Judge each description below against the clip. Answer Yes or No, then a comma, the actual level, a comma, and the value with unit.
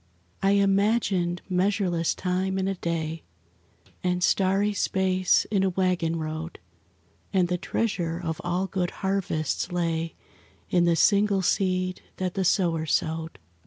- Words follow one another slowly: Yes, slow, 130 wpm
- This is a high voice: No, medium, 180 Hz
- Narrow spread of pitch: Yes, narrow, 2.3 semitones